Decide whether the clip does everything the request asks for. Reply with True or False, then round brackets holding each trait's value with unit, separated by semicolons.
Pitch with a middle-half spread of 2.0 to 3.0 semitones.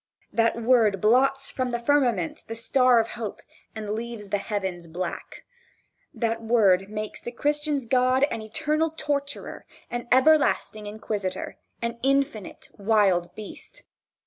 False (3.9 semitones)